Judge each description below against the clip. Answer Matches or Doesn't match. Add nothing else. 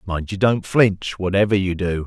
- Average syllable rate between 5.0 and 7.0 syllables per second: Doesn't match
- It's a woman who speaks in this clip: Doesn't match